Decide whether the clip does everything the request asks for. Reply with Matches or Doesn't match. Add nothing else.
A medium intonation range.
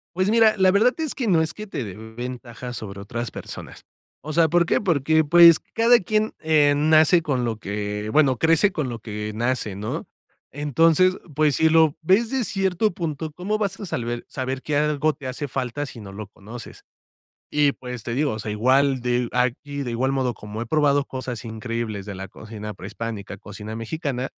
Doesn't match